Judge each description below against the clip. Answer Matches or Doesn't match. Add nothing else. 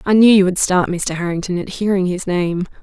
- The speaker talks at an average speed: Doesn't match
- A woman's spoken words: Matches